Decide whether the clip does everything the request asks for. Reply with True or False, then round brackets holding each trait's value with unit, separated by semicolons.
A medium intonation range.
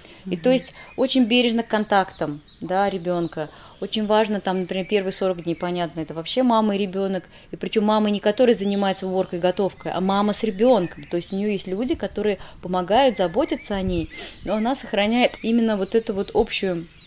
True (3.1 semitones)